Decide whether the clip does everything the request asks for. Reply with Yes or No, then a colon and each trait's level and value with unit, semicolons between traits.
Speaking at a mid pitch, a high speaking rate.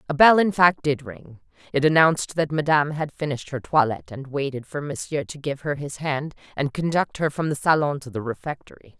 Yes: medium, 145 Hz; fast, 215 wpm